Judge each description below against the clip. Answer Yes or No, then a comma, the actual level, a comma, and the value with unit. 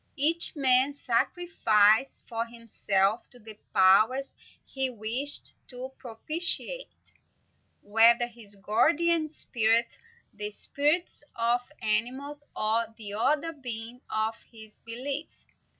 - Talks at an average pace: No, slow, 105 wpm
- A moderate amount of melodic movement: Yes, average, 4.4 semitones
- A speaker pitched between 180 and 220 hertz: No, high, 240 Hz